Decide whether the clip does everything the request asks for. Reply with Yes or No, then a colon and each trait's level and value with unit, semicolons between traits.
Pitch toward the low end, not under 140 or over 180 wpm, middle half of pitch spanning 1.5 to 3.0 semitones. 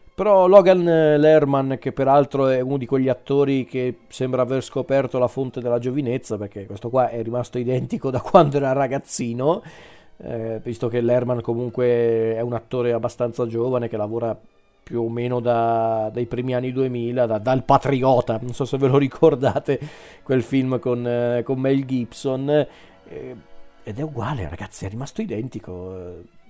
Yes: low, 125 Hz; average, 160 wpm; narrow, 2.6 semitones